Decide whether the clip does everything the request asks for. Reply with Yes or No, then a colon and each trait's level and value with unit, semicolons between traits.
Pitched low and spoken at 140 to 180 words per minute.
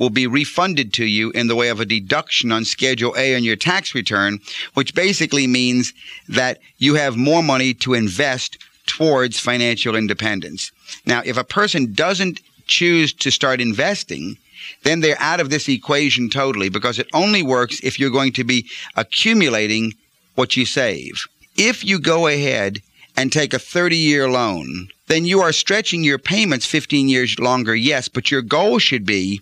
Yes: low, 130 Hz; average, 170 wpm